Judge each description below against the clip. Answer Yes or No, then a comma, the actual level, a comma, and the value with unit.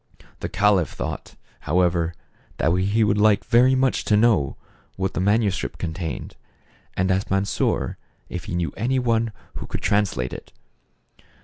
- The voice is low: Yes, low, 100 Hz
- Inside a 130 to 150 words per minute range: Yes, average, 145 wpm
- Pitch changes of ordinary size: Yes, average, 3.6 semitones